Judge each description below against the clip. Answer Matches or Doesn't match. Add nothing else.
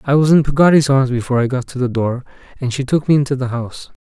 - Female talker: Doesn't match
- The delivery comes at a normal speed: Doesn't match